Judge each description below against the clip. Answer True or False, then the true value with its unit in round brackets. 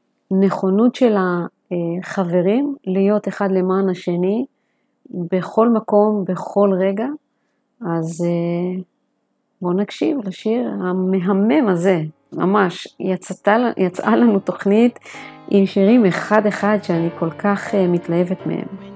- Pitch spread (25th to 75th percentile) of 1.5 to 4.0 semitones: True (2.6 semitones)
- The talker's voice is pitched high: True (195 Hz)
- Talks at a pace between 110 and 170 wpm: False (100 wpm)